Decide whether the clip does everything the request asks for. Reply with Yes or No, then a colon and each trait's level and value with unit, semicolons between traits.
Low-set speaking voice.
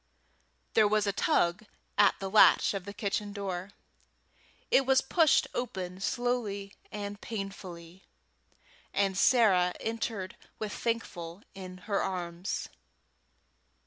No: high, 200 Hz